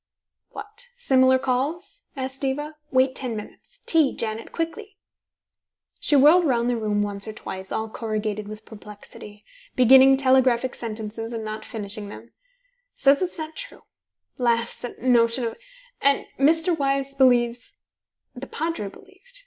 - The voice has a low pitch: No, very high, 255 Hz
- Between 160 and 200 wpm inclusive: No, average, 140 wpm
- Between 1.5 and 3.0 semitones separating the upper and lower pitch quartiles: No, average, 4.6 semitones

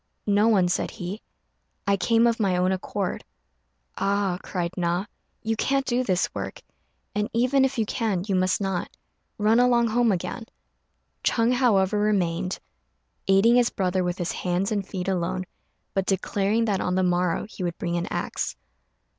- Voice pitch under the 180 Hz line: No, high, 195 Hz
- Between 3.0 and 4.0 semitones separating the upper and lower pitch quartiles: Yes, average, 3.7 semitones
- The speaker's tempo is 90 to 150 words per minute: No, average, 165 wpm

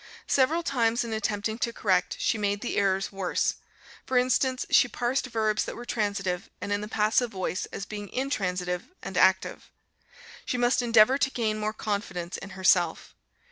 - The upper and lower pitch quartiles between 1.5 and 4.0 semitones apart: Yes, average, 3.6 semitones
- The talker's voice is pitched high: Yes, high, 215 Hz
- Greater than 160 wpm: Yes, average, 170 wpm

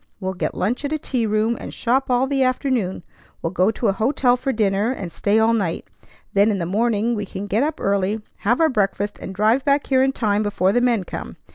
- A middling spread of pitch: Yes, average, 4.2 semitones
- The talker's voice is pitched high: Yes, high, 220 Hz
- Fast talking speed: Yes, fast, 235 wpm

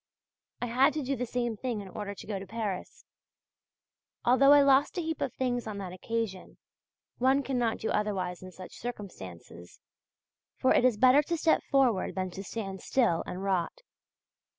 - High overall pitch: Yes, high, 230 Hz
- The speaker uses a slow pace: No, average, 175 wpm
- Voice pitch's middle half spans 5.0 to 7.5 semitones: Yes, average, 5.3 semitones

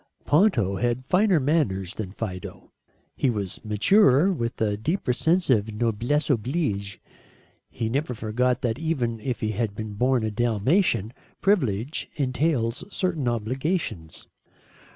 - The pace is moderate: No, slow, 130 wpm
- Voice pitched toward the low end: Yes, low, 120 Hz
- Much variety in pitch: Yes, wide, 5.8 semitones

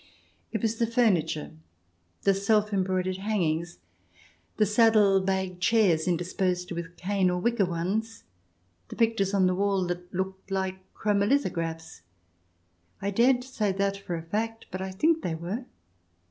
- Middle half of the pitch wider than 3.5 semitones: No, average, 3.2 semitones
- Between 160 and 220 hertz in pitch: Yes, high, 190 Hz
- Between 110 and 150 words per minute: Yes, average, 145 wpm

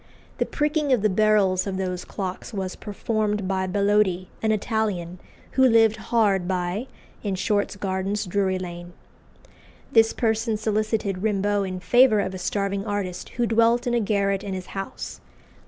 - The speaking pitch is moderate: No, high, 200 Hz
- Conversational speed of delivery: Yes, average, 155 wpm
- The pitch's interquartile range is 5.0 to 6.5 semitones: No, narrow, 2.6 semitones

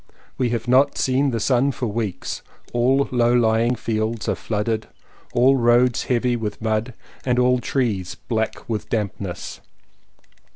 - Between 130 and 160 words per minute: Yes, average, 140 wpm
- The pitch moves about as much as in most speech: No, narrow, 2.3 semitones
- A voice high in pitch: No, low, 120 Hz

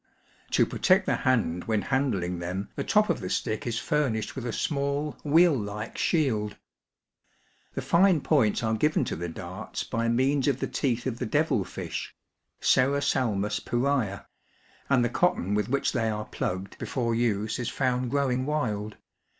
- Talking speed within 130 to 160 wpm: No, average, 170 wpm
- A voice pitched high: No, low, 120 Hz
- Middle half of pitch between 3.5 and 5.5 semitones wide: Yes, average, 4.9 semitones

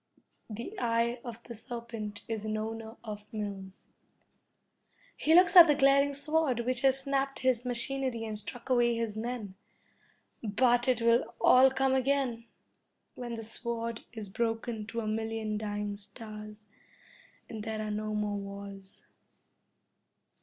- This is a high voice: Yes, high, 230 Hz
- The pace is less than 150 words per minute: Yes, average, 140 wpm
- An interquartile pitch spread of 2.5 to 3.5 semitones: Yes, average, 2.9 semitones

